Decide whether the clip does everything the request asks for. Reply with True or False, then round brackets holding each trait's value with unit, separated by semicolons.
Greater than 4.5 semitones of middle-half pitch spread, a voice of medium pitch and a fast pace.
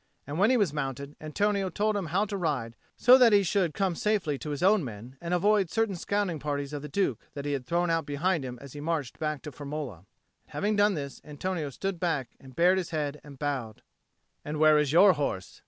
True (5.2 semitones; 155 Hz; 230 wpm)